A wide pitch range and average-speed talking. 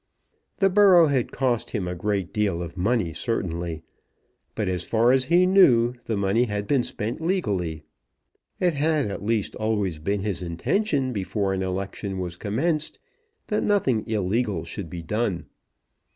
Yes: wide, 5.7 semitones; average, 155 wpm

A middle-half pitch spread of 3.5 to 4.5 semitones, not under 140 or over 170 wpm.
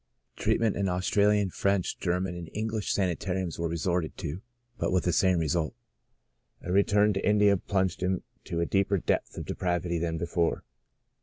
No: narrow, 2.6 semitones; average, 165 wpm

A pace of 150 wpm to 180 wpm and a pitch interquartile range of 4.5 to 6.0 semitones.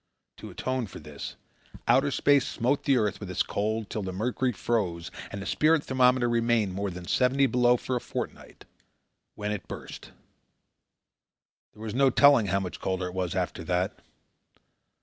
Yes: average, 170 wpm; average, 5.2 semitones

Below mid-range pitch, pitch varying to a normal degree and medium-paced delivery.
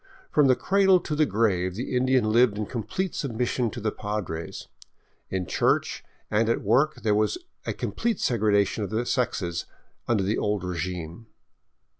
Yes: low, 110 Hz; average, 4.1 semitones; average, 160 wpm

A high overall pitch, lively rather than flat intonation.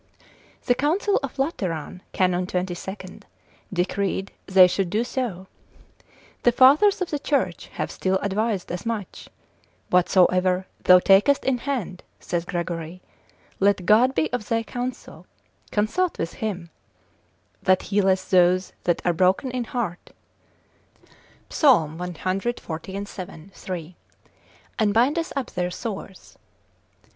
No: high, 195 Hz; average, 5.0 semitones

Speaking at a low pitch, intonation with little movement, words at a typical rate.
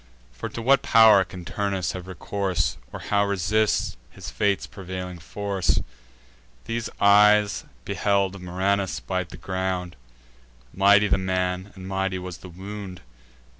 No: very low, 95 Hz; narrow, 1.8 semitones; slow, 130 wpm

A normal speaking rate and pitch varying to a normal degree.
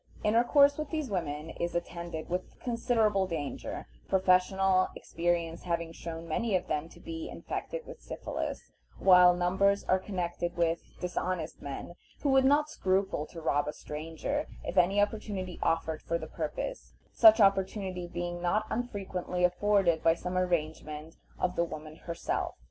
Yes: average, 150 wpm; average, 3.4 semitones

